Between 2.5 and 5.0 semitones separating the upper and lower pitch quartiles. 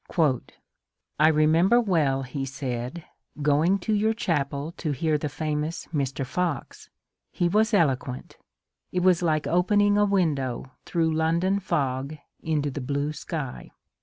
Yes: average, 4.3 semitones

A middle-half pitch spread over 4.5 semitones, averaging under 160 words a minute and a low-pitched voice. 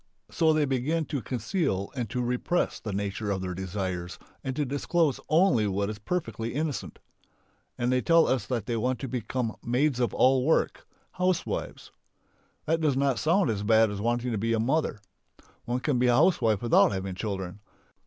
No: average, 5.2 semitones; average, 175 wpm; low, 120 Hz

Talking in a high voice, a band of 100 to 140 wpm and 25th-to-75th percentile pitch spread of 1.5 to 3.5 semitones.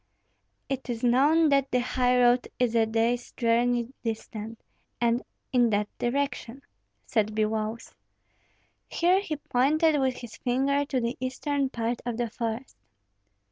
Yes: high, 245 Hz; slow, 135 wpm; average, 2.8 semitones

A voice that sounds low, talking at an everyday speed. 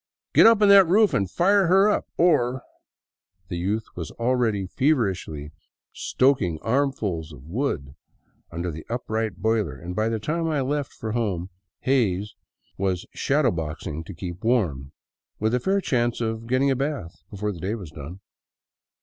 Yes: low, 110 Hz; average, 160 wpm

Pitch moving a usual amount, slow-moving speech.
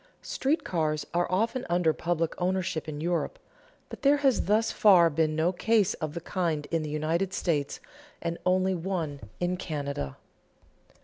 No: average, 3.2 semitones; average, 160 wpm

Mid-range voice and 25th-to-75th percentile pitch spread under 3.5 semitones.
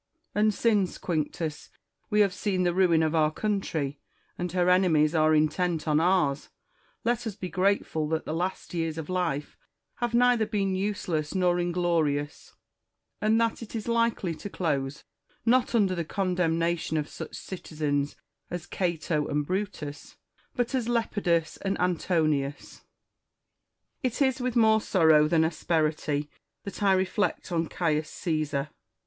No: medium, 175 Hz; average, 4.5 semitones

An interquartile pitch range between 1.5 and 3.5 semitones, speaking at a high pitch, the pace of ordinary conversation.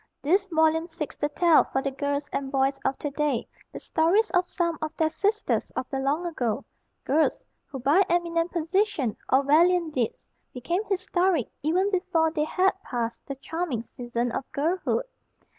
No: average, 4.5 semitones; very high, 315 Hz; average, 170 wpm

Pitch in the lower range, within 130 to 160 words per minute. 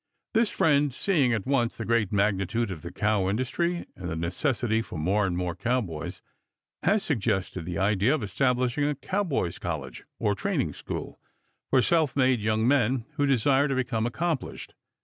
No: low, 120 Hz; average, 170 wpm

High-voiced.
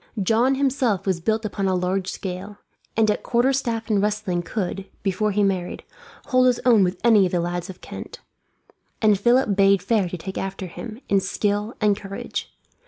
Yes: high, 200 Hz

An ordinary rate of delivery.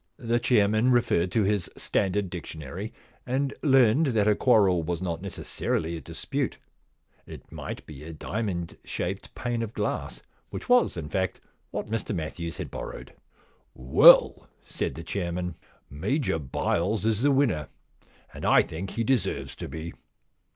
Yes: average, 155 wpm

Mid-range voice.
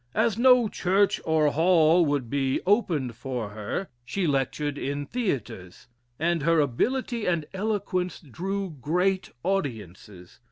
Yes: medium, 160 Hz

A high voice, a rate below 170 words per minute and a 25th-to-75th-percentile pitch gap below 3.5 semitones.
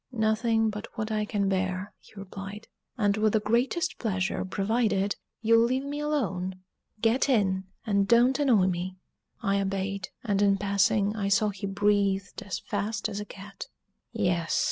Yes: high, 205 Hz; average, 160 wpm; narrow, 2.4 semitones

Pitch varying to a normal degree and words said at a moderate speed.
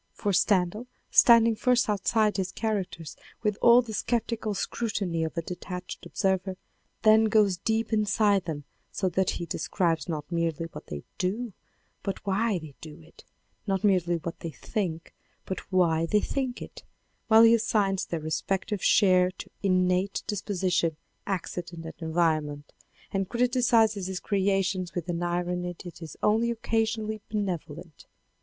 Yes: average, 3.8 semitones; average, 150 wpm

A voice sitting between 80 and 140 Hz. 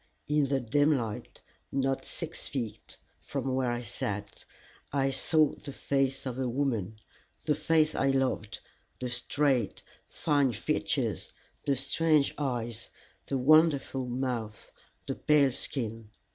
Yes: low, 135 Hz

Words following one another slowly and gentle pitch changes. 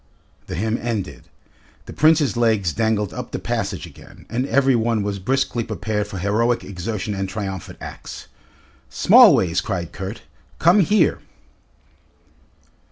No: slow, 130 wpm; average, 3.6 semitones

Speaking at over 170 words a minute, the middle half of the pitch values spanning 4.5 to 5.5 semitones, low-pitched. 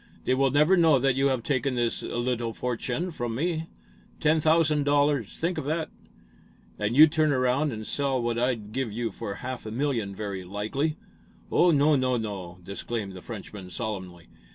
Yes: average, 180 wpm; average, 5.2 semitones; low, 125 Hz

